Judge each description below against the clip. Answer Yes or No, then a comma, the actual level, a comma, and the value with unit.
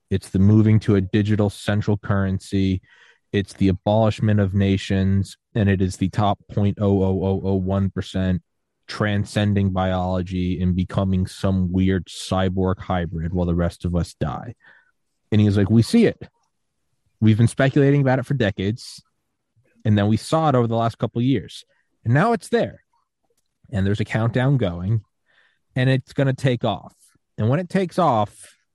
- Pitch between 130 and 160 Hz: No, low, 100 Hz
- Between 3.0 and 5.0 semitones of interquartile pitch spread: Yes, average, 3.3 semitones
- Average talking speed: Yes, average, 175 wpm